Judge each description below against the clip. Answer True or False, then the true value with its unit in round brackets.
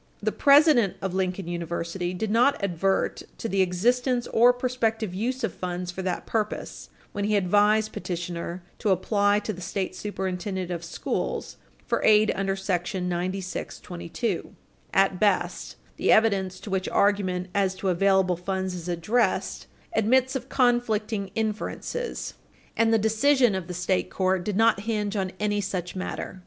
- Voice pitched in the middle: False (195 Hz)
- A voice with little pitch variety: False (3.3 semitones)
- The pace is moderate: True (150 wpm)